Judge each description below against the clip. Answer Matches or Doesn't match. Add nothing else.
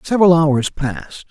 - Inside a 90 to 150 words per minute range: Matches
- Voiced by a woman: Doesn't match